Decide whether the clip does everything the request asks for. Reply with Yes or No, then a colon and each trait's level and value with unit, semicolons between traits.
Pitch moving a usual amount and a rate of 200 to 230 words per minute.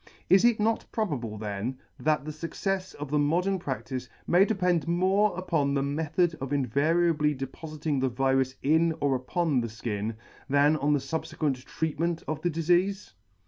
No: average, 4.5 semitones; average, 160 wpm